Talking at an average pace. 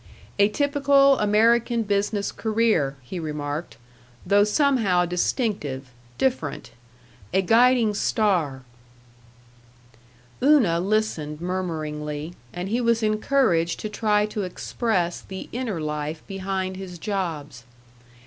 No: slow, 100 wpm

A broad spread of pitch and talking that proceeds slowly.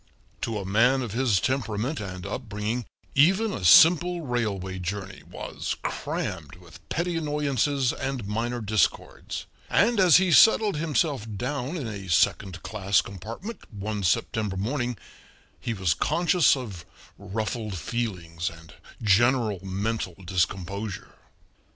Yes: wide, 5.9 semitones; slow, 125 wpm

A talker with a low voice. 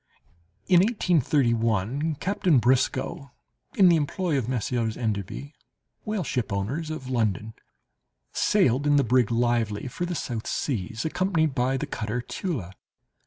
Yes: low, 130 Hz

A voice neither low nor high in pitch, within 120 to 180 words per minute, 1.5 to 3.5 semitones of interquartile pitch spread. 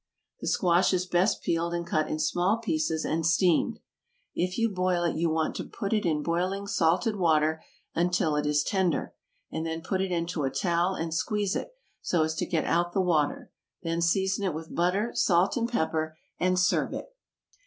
No: medium, 175 Hz; average, 195 wpm; average, 2.8 semitones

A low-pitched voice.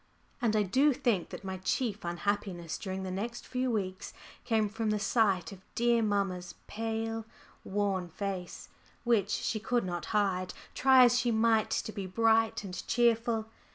No: high, 210 Hz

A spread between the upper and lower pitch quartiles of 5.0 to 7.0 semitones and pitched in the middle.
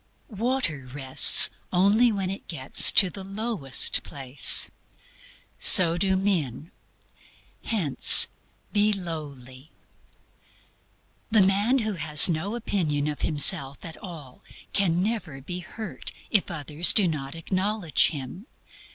Yes: wide, 5.6 semitones; medium, 175 Hz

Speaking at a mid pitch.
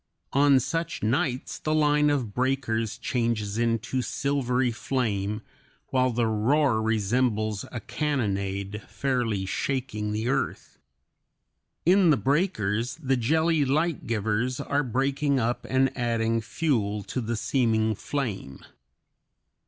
No: low, 125 Hz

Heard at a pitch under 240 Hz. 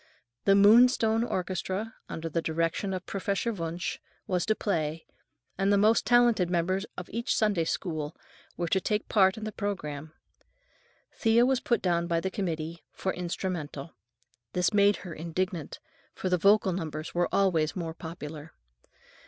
Yes: medium, 185 Hz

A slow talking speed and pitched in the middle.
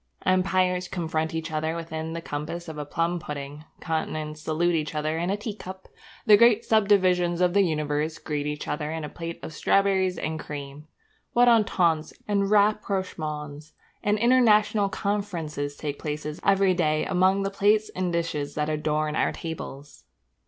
No: average, 160 wpm; medium, 165 Hz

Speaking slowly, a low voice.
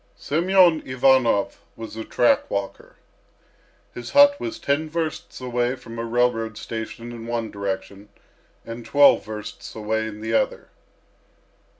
Yes: slow, 130 wpm; low, 115 Hz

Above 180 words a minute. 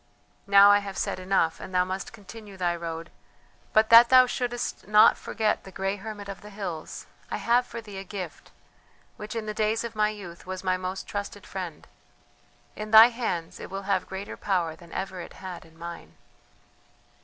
Yes: average, 190 wpm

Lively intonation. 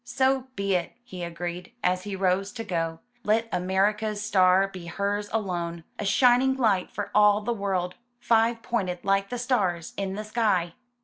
No: average, 3.5 semitones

